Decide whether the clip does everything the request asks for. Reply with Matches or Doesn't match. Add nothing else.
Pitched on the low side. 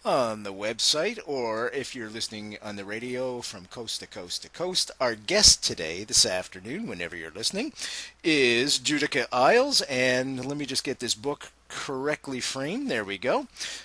Matches